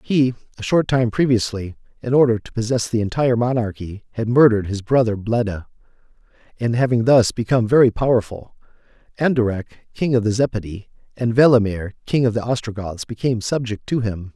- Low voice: Yes, low, 115 Hz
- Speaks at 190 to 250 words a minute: No, average, 160 wpm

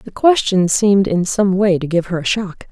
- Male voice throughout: No, female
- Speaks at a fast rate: Yes, fast, 245 wpm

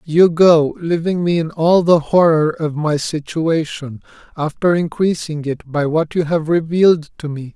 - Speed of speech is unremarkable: Yes, average, 165 wpm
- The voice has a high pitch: No, medium, 160 Hz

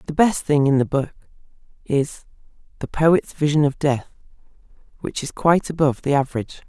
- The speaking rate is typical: Yes, average, 160 wpm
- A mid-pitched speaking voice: Yes, medium, 145 Hz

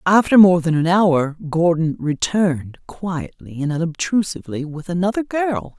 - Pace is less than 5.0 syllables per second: Yes, 4.6 syllables/s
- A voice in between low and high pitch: Yes, medium, 170 Hz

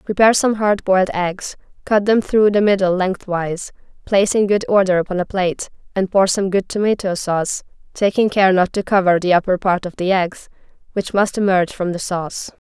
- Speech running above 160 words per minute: Yes, average, 195 wpm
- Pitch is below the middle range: No, high, 190 Hz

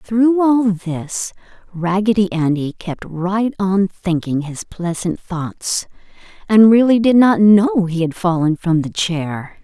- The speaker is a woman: Yes, female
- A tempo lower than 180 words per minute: Yes, average, 145 wpm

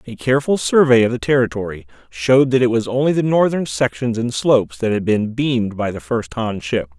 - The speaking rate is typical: No, fast, 215 wpm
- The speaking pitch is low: Yes, low, 120 Hz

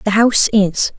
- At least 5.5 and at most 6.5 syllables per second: No, 5.1 syllables/s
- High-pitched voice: Yes, high, 210 Hz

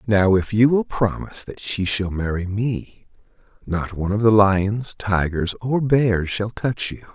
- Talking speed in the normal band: Yes, average, 175 wpm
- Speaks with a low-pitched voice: Yes, low, 105 Hz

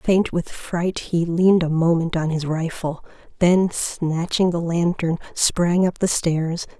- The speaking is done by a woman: Yes, female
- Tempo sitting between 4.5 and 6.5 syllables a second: No, 3.7 syllables/s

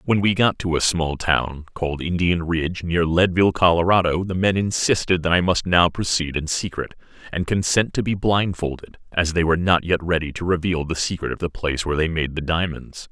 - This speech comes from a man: Yes, male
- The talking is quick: Yes, fast, 210 wpm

